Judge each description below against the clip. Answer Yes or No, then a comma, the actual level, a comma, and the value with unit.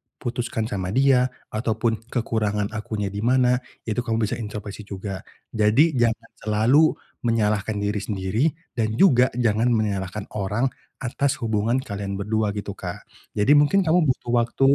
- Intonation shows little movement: No, average, 3.1 semitones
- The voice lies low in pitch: Yes, low, 110 Hz